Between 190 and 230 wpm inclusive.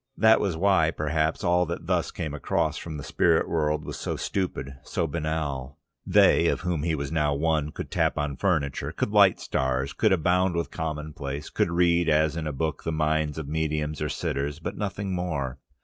Yes: average, 195 wpm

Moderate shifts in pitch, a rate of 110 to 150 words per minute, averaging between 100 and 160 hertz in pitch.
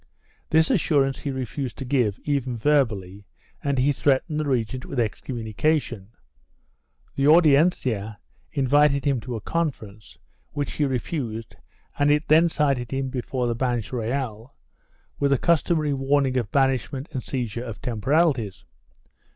Yes: average, 3.7 semitones; average, 145 wpm; low, 135 Hz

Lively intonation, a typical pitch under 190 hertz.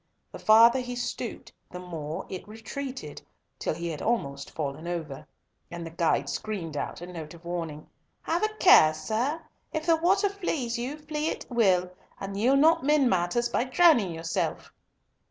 No: wide, 8.5 semitones; high, 215 Hz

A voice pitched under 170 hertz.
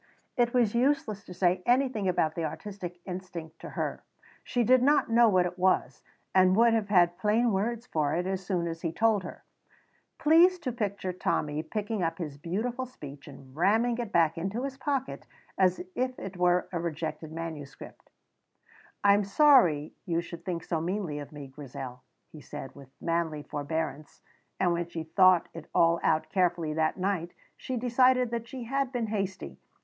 No: medium, 185 Hz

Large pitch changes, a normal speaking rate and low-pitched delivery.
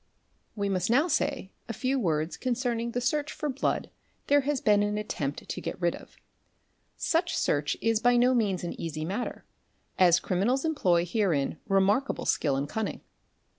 No: wide, 6.4 semitones; average, 170 wpm; high, 210 Hz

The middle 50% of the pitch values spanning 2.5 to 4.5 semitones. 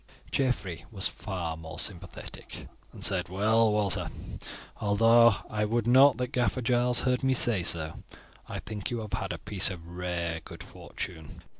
No: average, 4.9 semitones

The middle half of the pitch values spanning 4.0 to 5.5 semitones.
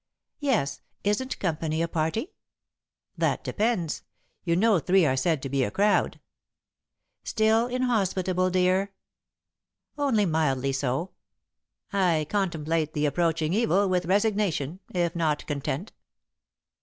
Yes: average, 4.7 semitones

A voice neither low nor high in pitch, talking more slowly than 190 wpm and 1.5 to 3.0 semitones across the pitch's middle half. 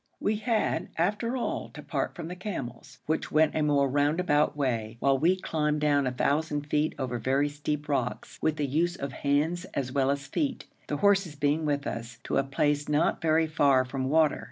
No: medium, 145 Hz; average, 195 wpm; narrow, 2.6 semitones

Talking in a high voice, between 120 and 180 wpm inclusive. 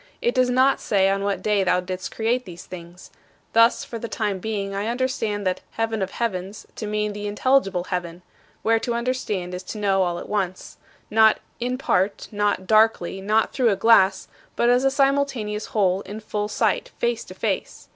No: high, 210 Hz; average, 190 wpm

